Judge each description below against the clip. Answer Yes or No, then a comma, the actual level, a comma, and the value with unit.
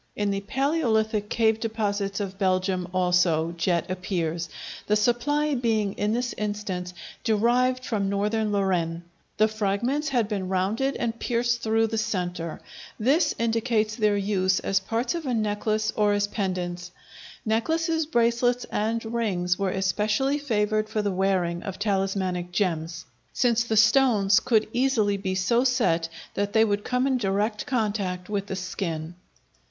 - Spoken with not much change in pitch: No, average, 3.5 semitones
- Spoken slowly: No, average, 145 wpm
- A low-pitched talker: No, high, 210 Hz